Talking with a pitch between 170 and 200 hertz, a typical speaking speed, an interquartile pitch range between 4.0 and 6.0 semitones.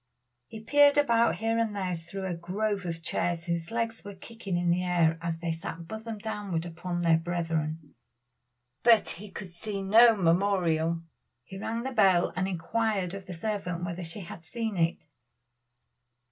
Yes: medium, 185 Hz; average, 170 wpm; average, 4.3 semitones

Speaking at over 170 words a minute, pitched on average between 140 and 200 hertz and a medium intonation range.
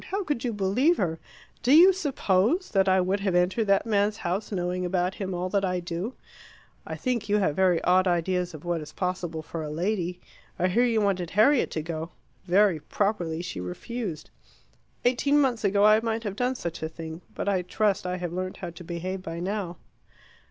Yes: average, 200 wpm; medium, 185 Hz; average, 3.5 semitones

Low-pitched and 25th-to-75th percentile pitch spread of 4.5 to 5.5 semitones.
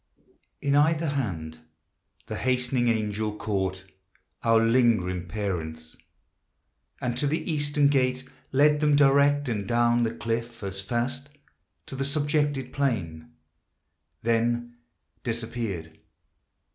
Yes: low, 120 Hz; average, 5.2 semitones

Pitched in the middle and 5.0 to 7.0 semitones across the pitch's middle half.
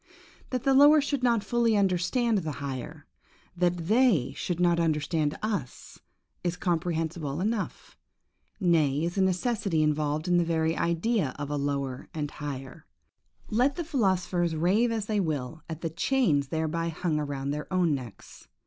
Yes: medium, 170 Hz; wide, 5.4 semitones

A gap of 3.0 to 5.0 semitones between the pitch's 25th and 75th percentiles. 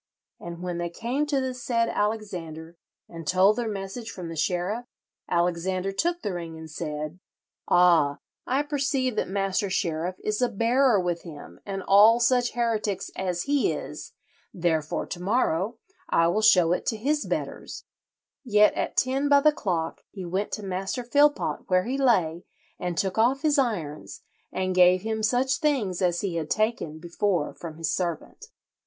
No: wide, 5.6 semitones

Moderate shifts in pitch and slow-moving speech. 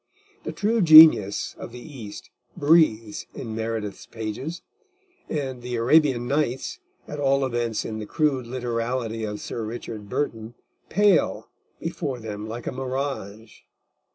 Yes: average, 4.2 semitones; slow, 130 wpm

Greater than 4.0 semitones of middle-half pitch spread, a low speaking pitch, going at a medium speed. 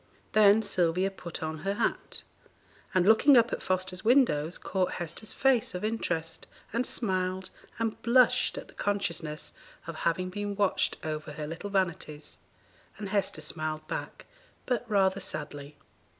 No: average, 4.5 semitones; medium, 185 Hz; average, 145 wpm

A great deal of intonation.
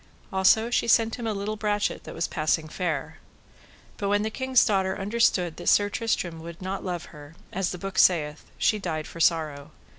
No: average, 4.2 semitones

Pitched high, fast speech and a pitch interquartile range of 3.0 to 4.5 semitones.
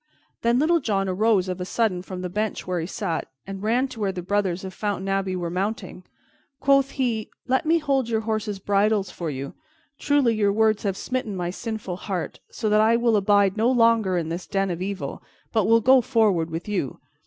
Yes: high, 205 Hz; fast, 210 wpm; average, 3.7 semitones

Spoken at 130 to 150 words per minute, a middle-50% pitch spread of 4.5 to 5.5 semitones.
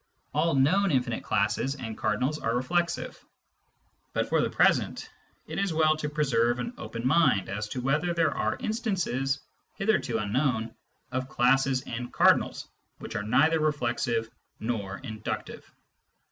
Yes: average, 140 wpm; average, 5.1 semitones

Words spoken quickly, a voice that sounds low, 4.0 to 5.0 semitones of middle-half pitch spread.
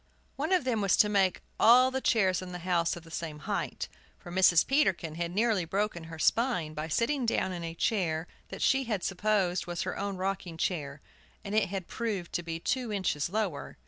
No: fast, 210 wpm; medium, 185 Hz; average, 4.3 semitones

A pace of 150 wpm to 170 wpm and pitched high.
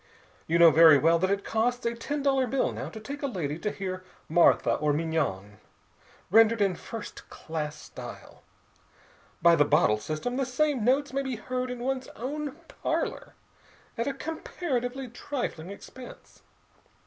Yes: average, 160 wpm; high, 225 Hz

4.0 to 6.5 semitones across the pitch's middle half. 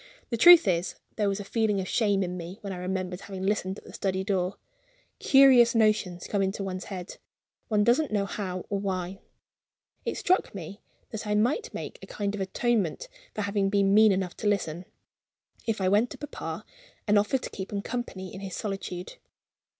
No: narrow, 2.4 semitones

